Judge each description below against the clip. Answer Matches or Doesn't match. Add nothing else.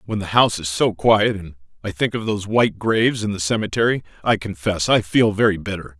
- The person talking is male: Matches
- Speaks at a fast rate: Matches